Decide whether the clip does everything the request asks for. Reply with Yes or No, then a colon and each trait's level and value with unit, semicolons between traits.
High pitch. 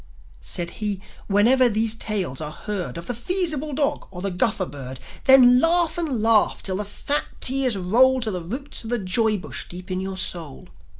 Yes: high, 215 Hz